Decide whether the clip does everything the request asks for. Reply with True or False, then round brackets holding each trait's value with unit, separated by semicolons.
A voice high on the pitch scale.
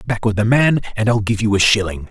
False (110 Hz)